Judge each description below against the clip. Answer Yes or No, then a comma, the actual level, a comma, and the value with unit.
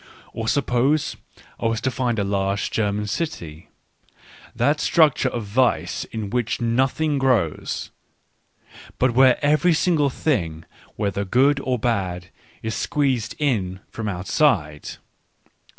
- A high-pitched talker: No, low, 120 Hz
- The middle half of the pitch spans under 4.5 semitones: No, average, 5.3 semitones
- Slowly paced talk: Yes, slow, 130 wpm